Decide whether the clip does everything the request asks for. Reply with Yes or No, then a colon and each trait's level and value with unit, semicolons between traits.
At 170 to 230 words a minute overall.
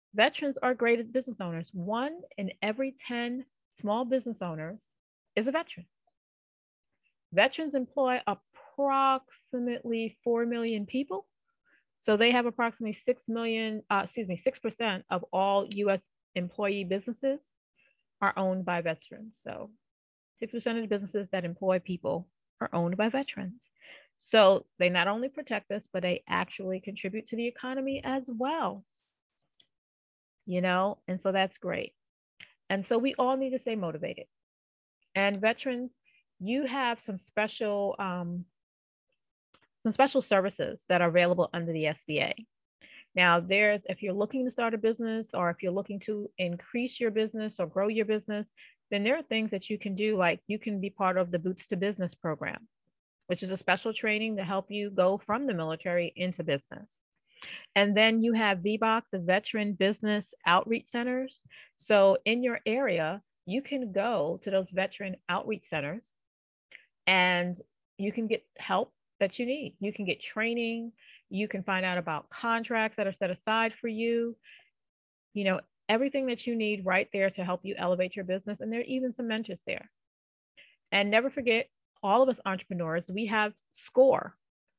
No: average, 160 wpm